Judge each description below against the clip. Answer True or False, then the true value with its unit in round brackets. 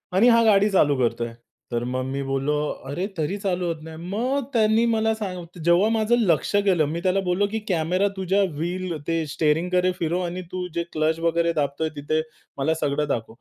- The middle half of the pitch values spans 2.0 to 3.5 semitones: False (4.3 semitones)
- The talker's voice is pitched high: False (170 Hz)